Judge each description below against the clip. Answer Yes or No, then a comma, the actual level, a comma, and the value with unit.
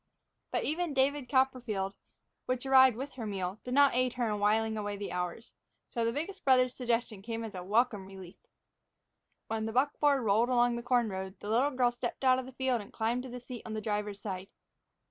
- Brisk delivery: Yes, fast, 210 wpm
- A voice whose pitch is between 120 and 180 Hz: No, high, 235 Hz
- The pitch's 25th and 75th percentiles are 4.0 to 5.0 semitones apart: No, average, 3.6 semitones